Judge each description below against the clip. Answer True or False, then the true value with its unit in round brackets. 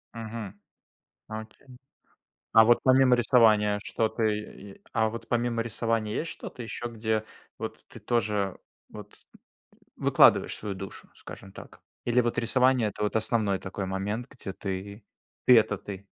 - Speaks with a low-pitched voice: True (110 Hz)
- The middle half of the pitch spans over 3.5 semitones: False (2.4 semitones)